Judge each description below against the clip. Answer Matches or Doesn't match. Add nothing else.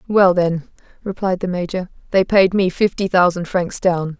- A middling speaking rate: Matches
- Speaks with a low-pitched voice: Doesn't match